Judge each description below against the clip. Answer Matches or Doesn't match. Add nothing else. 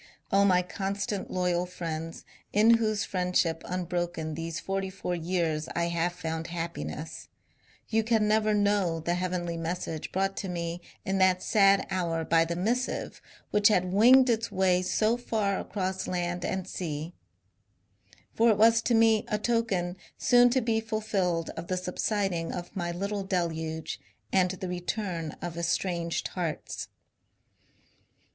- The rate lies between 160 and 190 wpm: Doesn't match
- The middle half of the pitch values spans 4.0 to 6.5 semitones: Doesn't match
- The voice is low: Doesn't match